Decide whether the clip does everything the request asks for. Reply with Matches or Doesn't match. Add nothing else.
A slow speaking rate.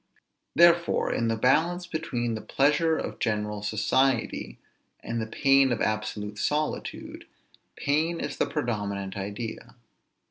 Matches